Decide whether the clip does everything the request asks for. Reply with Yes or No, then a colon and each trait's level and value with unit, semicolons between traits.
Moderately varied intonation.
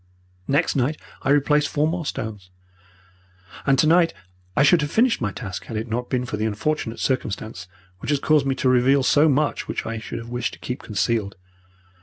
Yes: average, 4.9 semitones